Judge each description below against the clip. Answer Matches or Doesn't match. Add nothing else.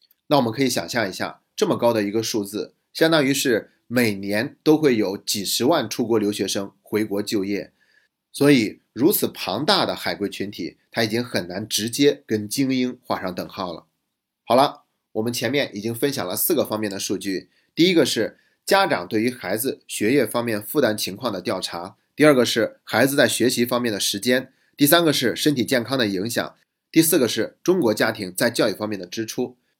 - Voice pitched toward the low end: Matches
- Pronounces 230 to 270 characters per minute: Doesn't match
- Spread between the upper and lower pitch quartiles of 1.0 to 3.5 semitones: Doesn't match